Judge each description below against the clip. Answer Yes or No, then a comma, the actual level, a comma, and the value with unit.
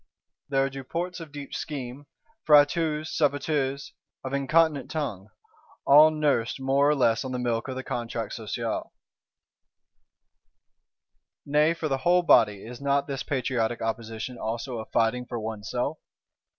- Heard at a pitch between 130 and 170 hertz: Yes, low, 135 Hz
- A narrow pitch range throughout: No, average, 3.8 semitones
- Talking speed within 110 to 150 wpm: Yes, slow, 135 wpm